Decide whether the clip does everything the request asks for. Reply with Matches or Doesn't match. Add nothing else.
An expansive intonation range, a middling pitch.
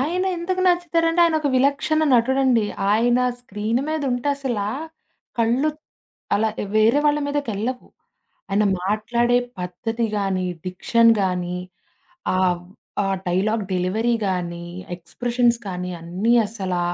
Doesn't match